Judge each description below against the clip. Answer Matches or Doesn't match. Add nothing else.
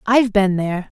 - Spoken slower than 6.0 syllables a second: Doesn't match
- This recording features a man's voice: Doesn't match